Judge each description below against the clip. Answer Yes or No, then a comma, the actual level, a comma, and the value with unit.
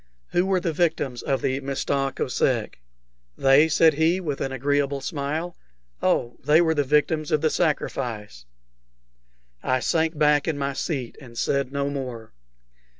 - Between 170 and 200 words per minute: No, average, 150 wpm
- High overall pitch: No, medium, 140 Hz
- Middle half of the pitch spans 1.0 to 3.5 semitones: Yes, average, 3.0 semitones